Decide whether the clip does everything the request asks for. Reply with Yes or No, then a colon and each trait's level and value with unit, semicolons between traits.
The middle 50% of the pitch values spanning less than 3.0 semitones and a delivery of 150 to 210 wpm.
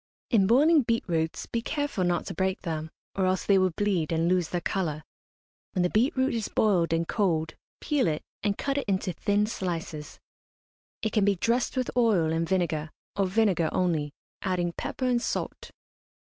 No: average, 5.1 semitones; average, 185 wpm